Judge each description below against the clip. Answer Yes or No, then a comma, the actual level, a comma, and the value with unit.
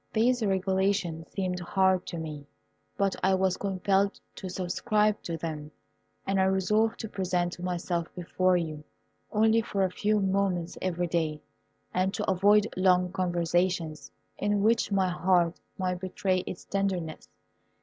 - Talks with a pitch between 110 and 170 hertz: No, medium, 185 Hz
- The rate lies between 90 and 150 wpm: Yes, average, 140 wpm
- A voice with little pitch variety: Yes, narrow, 2.1 semitones